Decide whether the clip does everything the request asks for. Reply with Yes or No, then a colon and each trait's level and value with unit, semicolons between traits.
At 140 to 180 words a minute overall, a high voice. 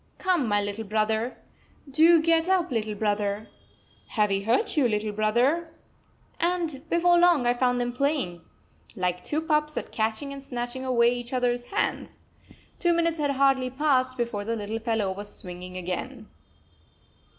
Yes: average, 155 wpm; high, 245 Hz